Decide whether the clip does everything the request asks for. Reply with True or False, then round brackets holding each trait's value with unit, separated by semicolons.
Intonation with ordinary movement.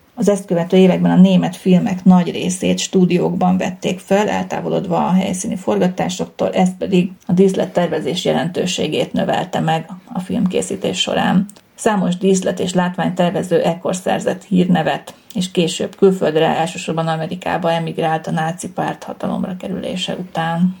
False (2.3 semitones)